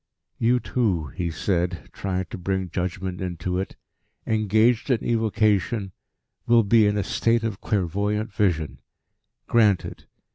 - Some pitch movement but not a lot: Yes, average, 3.4 semitones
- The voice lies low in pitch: Yes, low, 100 Hz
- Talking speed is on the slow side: Yes, slow, 130 wpm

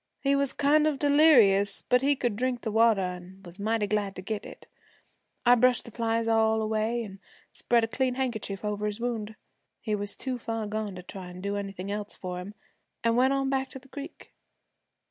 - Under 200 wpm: No, fast, 205 wpm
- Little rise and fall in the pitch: No, average, 3.8 semitones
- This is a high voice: Yes, high, 225 Hz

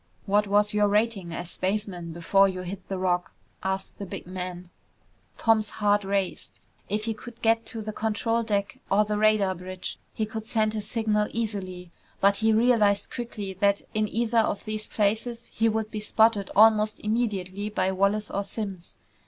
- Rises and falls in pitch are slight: Yes, narrow, 2.3 semitones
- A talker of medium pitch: No, high, 210 Hz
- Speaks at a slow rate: No, average, 175 wpm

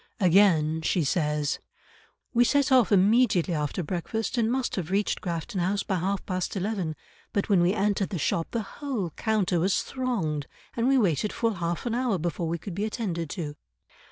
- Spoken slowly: No, average, 185 wpm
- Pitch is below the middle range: No, high, 190 Hz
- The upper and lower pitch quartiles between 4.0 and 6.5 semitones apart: Yes, average, 4.7 semitones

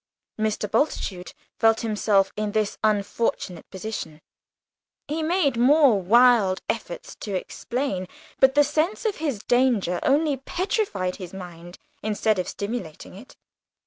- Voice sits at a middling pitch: No, high, 220 Hz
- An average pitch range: No, wide, 6.1 semitones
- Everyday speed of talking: No, slow, 125 wpm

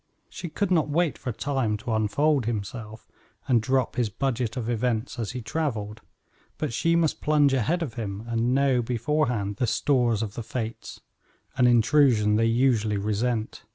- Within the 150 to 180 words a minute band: Yes, average, 165 wpm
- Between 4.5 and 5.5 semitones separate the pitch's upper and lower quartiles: No, average, 3.8 semitones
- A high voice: No, low, 120 Hz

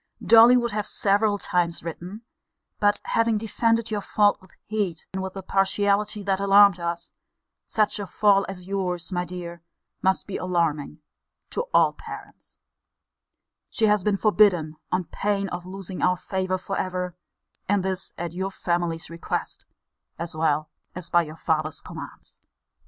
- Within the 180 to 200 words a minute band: No, average, 150 wpm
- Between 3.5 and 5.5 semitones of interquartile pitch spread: No, average, 3.0 semitones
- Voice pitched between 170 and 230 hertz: Yes, high, 190 Hz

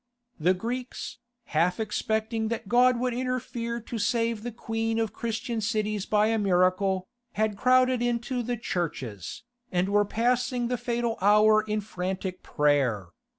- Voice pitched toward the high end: Yes, high, 220 Hz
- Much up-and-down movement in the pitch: No, average, 3.6 semitones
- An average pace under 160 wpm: Yes, average, 145 wpm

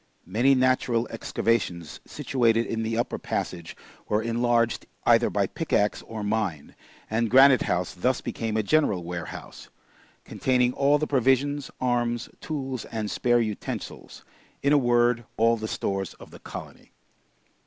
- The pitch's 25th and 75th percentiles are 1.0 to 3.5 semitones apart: Yes, average, 2.9 semitones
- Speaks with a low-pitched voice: Yes, low, 115 Hz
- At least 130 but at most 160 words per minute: Yes, average, 145 wpm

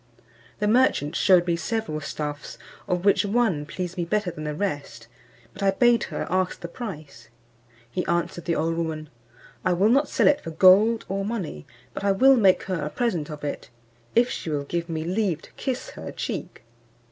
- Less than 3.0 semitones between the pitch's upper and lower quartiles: No, average, 4.8 semitones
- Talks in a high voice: No, medium, 180 Hz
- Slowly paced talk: No, average, 195 wpm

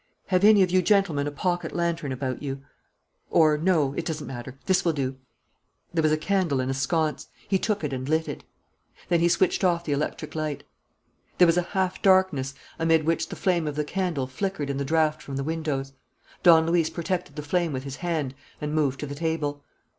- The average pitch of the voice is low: No, medium, 160 Hz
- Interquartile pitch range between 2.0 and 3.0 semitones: No, average, 3.7 semitones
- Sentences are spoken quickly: Yes, fast, 210 wpm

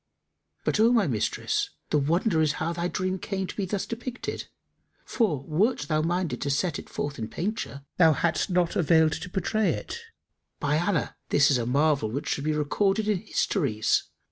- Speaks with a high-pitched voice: No, medium, 165 Hz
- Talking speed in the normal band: Yes, average, 185 wpm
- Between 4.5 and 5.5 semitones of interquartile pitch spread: Yes, average, 4.9 semitones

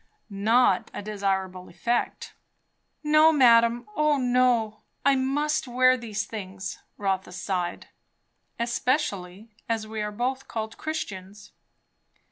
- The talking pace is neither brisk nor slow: No, slow, 105 wpm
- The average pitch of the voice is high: Yes, high, 230 Hz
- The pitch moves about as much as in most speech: Yes, average, 4.3 semitones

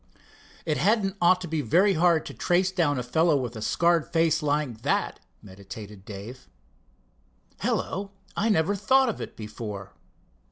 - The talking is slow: No, average, 155 wpm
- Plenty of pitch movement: Yes, wide, 8.1 semitones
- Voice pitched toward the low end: No, medium, 160 Hz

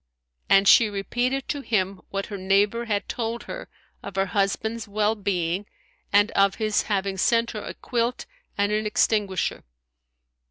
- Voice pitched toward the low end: No, high, 205 Hz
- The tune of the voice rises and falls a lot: No, narrow, 2.4 semitones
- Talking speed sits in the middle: Yes, average, 155 wpm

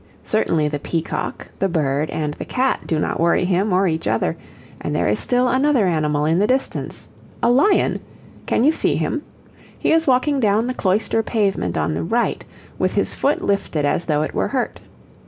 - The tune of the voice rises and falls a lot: Yes, wide, 8.3 semitones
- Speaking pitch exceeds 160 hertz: Yes, high, 190 Hz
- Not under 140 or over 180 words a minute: No, average, 190 wpm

